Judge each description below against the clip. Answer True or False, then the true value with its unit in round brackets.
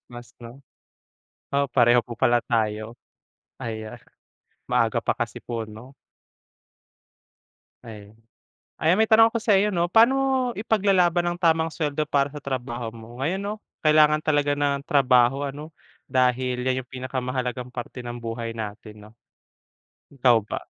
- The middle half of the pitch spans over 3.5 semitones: True (4.7 semitones)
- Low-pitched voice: True (130 Hz)